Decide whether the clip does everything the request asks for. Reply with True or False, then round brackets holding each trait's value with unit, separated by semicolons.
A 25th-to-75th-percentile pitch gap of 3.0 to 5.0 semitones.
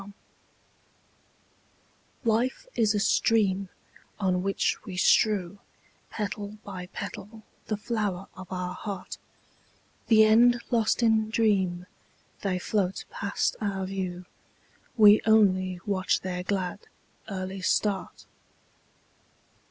False (2.6 semitones)